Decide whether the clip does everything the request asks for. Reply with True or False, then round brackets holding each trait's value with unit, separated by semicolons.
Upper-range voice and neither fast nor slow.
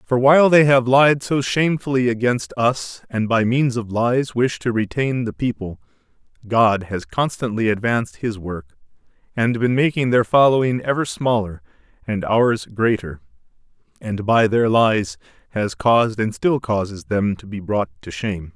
False (115 Hz; 160 wpm)